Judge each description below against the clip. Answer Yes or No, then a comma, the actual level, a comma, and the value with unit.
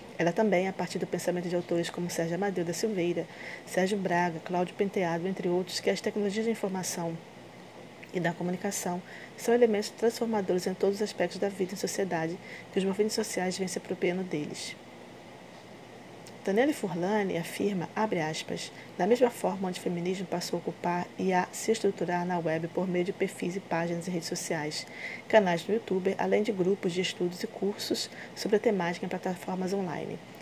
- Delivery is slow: No, average, 180 wpm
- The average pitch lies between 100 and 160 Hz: No, medium, 185 Hz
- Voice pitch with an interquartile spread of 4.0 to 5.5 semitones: No, narrow, 2.5 semitones